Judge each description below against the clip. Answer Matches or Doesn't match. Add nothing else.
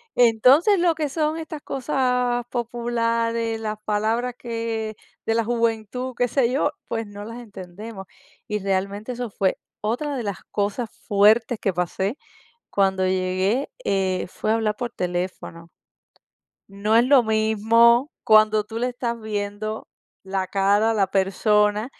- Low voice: Doesn't match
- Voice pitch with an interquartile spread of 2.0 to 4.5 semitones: Matches